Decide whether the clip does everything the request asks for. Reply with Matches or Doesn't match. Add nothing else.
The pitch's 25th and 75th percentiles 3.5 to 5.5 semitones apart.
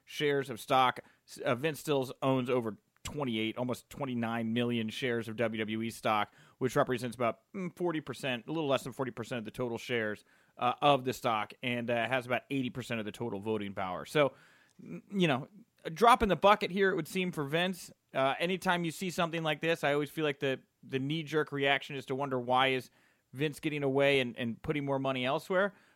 Matches